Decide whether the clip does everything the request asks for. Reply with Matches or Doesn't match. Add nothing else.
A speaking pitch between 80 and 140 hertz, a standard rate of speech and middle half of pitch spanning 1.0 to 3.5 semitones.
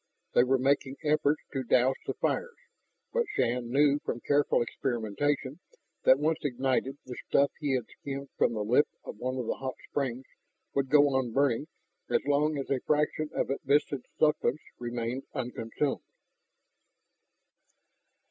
Matches